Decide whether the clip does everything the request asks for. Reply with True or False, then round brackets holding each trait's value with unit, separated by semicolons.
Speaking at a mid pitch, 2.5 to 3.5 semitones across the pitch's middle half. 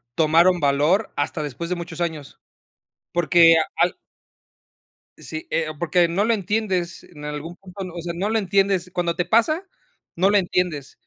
True (175 Hz; 3.0 semitones)